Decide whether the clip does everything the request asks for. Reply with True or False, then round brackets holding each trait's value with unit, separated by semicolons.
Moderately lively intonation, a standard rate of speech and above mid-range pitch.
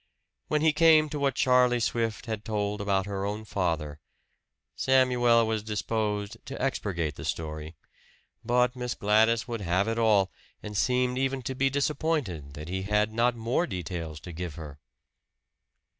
False (4.7 semitones; 160 wpm; 110 Hz)